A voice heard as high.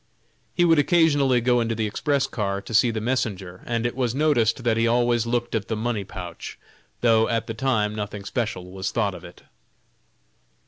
No: low, 115 Hz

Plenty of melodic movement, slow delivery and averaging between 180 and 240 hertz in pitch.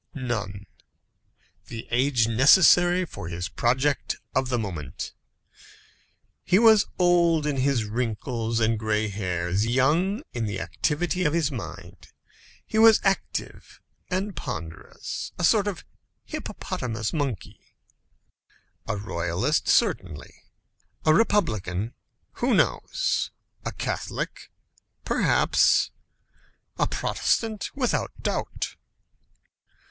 No: wide, 8.9 semitones; slow, 100 wpm; low, 125 Hz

